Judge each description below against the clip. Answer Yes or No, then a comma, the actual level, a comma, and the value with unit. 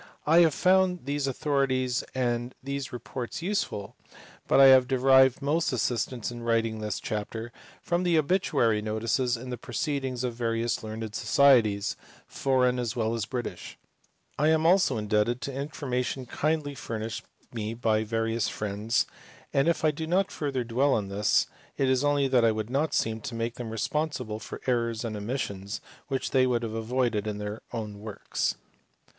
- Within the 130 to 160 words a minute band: No, average, 170 wpm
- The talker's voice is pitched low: Yes, low, 125 Hz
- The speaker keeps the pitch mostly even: No, average, 3.8 semitones